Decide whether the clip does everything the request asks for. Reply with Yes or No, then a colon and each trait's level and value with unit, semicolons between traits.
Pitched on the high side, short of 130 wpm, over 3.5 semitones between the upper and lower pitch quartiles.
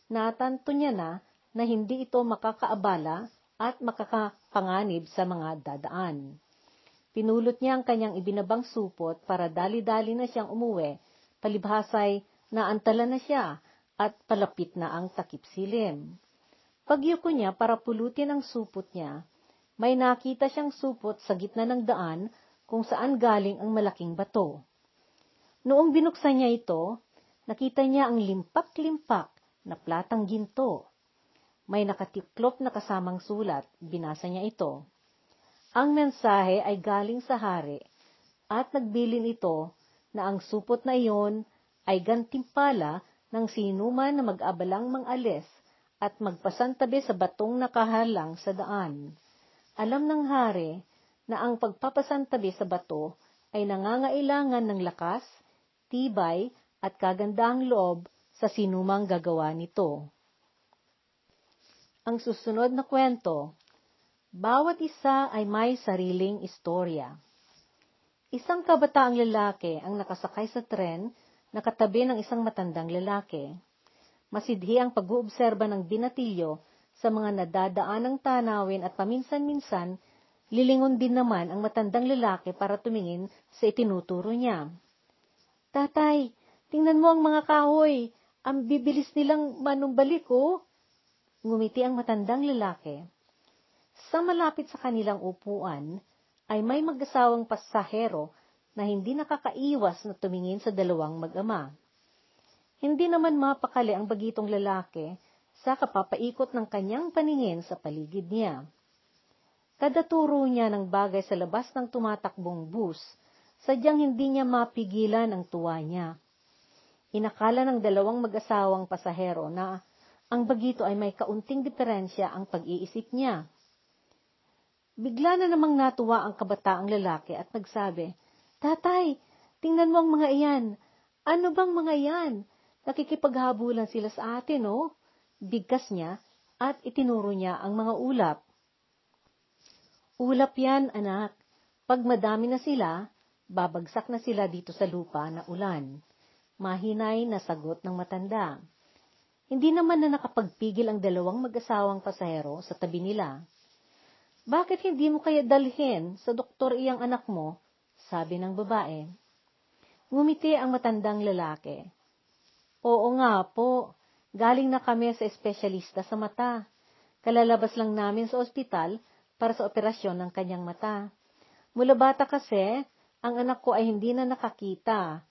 Yes: high, 220 Hz; average, 120 wpm; average, 5.1 semitones